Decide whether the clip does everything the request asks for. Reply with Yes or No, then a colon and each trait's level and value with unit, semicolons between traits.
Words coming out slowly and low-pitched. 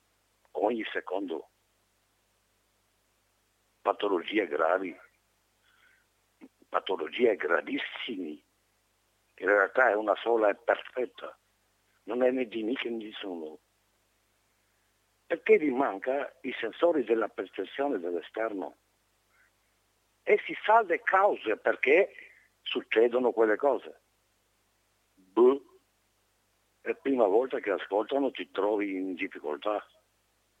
Yes: slow, 95 wpm; low, 115 Hz